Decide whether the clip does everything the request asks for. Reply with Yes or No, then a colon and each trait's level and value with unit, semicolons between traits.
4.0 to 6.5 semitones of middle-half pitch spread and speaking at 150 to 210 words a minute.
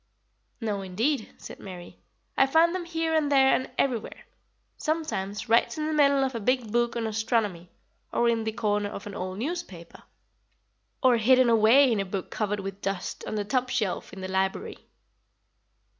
Yes: average, 5.0 semitones; average, 175 wpm